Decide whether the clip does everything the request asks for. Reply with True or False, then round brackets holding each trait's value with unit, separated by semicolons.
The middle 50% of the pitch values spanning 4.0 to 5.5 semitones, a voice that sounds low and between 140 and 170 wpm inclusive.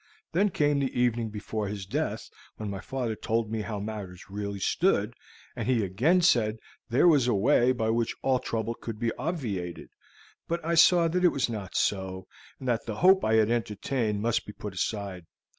False (4.3 semitones; 115 Hz; 195 wpm)